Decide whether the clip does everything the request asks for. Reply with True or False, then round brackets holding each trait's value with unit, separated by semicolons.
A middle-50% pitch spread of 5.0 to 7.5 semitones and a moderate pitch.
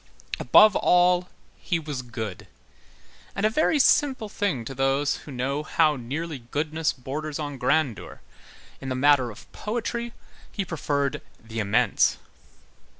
True (5.4 semitones; 145 Hz)